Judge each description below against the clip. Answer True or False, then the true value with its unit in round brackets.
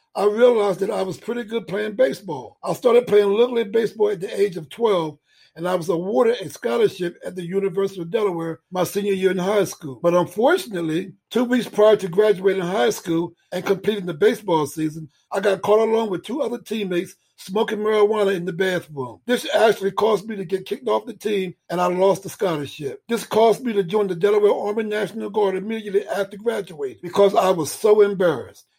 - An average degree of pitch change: True (3.2 semitones)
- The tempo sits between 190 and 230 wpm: True (200 wpm)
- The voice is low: False (200 Hz)